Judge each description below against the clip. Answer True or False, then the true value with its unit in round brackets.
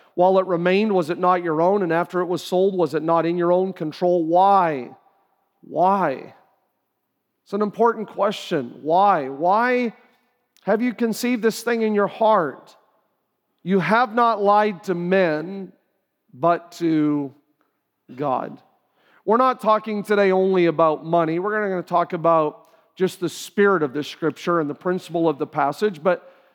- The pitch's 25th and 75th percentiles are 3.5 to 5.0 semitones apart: True (3.9 semitones)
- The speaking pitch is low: False (180 Hz)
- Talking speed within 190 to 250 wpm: False (160 wpm)